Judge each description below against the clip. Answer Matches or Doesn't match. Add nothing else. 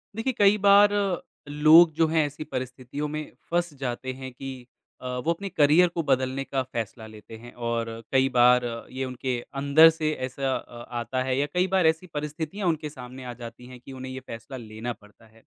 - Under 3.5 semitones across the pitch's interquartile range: Doesn't match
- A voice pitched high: Doesn't match